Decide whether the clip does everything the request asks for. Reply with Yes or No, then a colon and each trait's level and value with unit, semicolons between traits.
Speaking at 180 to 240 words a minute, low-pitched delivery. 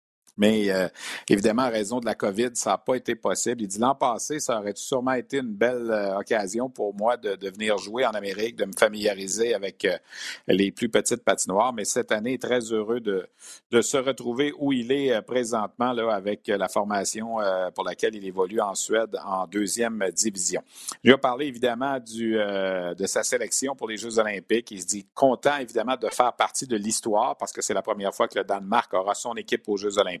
Yes: average, 215 wpm; low, 110 Hz